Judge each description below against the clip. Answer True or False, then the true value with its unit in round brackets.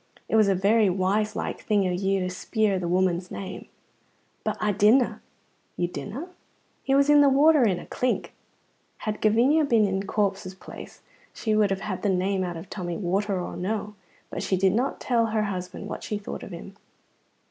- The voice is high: True (200 Hz)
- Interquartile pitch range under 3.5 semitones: True (2.9 semitones)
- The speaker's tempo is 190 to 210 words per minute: True (200 wpm)